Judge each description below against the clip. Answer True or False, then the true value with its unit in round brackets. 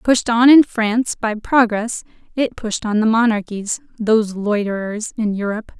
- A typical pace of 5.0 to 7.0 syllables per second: False (4.7 syllables/s)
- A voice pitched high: True (220 Hz)